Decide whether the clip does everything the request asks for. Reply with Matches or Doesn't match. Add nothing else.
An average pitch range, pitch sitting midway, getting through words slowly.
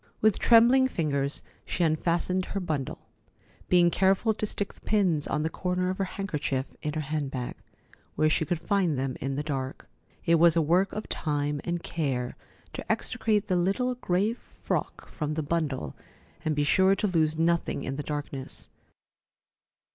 Doesn't match